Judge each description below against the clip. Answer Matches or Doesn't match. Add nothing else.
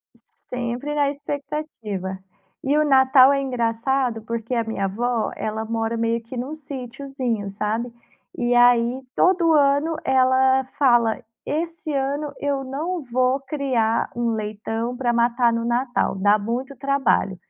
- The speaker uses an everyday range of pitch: Matches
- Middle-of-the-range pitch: Doesn't match